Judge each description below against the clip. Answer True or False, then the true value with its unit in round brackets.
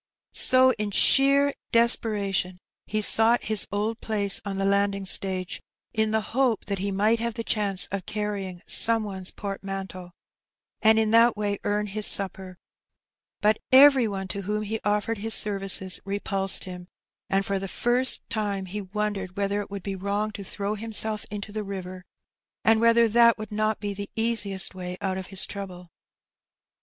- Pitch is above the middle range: True (205 Hz)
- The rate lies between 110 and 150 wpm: False (170 wpm)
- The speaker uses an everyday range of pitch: False (2.1 semitones)